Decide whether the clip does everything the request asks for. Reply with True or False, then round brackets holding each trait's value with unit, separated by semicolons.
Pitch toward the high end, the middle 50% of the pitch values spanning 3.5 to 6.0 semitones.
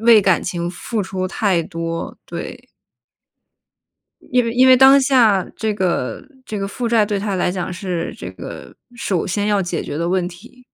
True (195 Hz; 4.4 semitones)